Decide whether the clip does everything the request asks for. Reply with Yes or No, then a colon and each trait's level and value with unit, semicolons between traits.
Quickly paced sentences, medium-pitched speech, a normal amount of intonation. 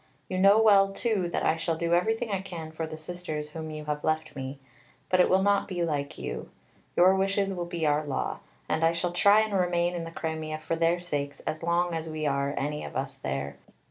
Yes: fast, 230 wpm; medium, 165 Hz; average, 3.1 semitones